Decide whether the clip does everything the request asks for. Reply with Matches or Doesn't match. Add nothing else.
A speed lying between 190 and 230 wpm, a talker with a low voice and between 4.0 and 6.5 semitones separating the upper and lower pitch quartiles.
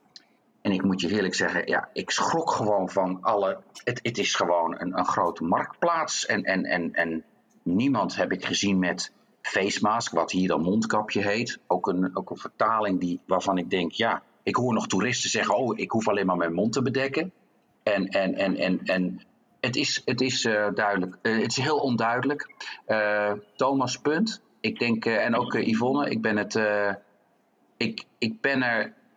Doesn't match